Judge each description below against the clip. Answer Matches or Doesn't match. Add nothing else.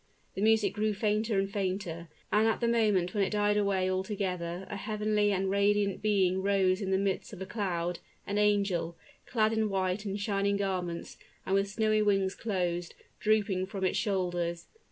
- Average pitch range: Doesn't match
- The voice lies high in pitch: Matches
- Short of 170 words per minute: Doesn't match